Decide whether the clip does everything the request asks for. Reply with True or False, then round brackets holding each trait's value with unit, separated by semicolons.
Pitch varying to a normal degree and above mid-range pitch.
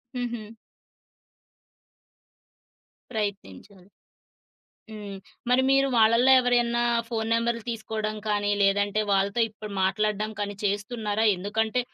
False (2.2 semitones; 215 Hz)